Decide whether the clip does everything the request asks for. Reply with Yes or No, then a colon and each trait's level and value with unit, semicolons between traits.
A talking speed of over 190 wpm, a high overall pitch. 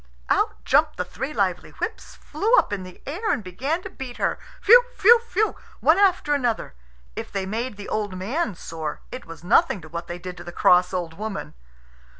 Yes: average, 200 wpm; high, 215 Hz